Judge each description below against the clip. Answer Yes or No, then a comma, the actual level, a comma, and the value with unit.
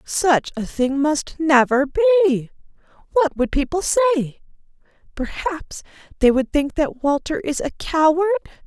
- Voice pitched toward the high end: Yes, very high, 310 Hz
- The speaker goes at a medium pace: No, slow, 130 wpm